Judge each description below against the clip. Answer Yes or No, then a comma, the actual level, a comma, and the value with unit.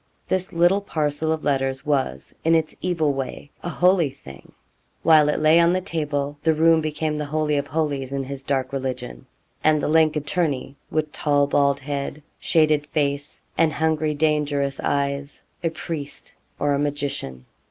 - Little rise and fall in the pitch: Yes, narrow, 2.1 semitones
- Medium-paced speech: Yes, average, 165 wpm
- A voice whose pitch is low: No, medium, 150 Hz